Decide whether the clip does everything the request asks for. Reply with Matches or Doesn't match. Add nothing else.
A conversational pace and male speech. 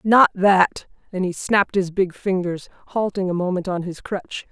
Doesn't match